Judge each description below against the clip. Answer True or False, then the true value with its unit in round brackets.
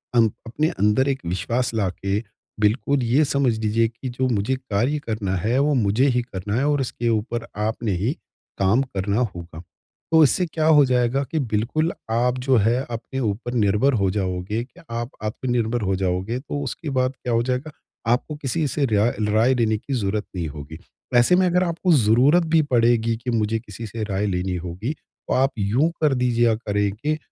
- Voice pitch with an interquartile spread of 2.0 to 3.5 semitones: False (4.2 semitones)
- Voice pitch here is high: False (120 Hz)